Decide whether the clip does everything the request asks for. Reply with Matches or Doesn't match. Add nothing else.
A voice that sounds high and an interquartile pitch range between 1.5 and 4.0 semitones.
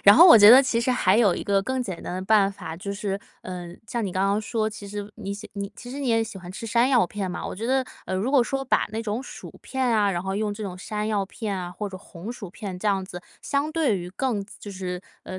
Matches